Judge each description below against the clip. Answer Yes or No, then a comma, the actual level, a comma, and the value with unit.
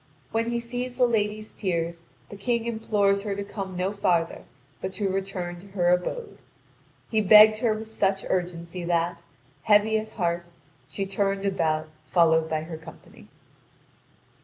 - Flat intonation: No, average, 3.7 semitones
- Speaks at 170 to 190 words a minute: No, average, 155 wpm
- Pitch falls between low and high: No, high, 195 Hz